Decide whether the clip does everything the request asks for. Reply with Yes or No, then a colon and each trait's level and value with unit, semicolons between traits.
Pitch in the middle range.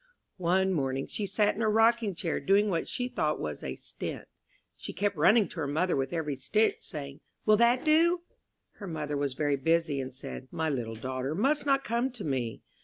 Yes: medium, 170 Hz